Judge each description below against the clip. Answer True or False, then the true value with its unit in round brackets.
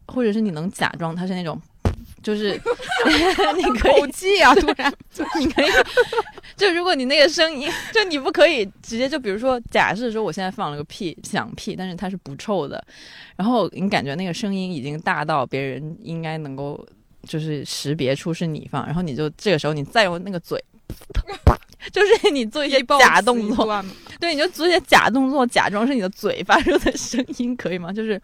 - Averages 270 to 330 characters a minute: True (285 characters per minute)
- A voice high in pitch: True (210 Hz)